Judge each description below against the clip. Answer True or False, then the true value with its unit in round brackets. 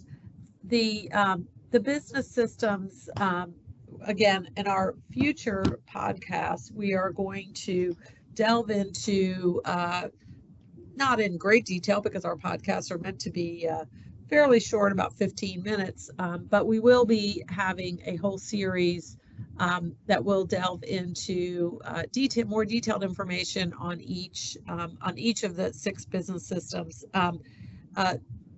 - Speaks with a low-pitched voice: False (190 Hz)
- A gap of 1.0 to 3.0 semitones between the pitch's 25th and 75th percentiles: False (3.4 semitones)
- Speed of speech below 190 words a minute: True (140 wpm)